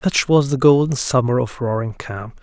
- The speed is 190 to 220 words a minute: Yes, average, 200 wpm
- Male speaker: Yes, male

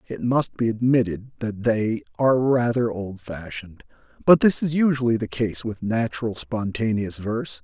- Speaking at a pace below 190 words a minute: Yes, average, 150 wpm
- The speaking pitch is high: No, low, 110 Hz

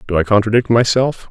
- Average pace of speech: Yes, average, 185 wpm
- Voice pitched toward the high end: No, low, 115 Hz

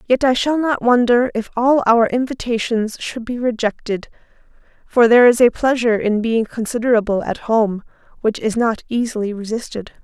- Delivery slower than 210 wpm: Yes, average, 160 wpm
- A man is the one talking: No, female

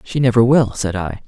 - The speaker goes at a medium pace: No, fast, 235 wpm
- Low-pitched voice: Yes, low, 115 Hz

